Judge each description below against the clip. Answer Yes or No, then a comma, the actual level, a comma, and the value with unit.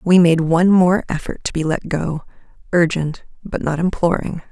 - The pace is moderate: Yes, average, 175 wpm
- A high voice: No, medium, 170 Hz